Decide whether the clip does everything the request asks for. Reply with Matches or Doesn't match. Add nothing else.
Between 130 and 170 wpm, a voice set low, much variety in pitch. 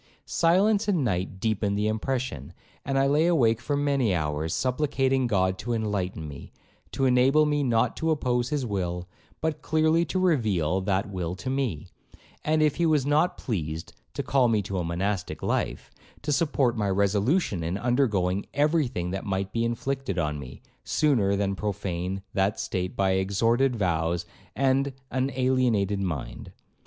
Matches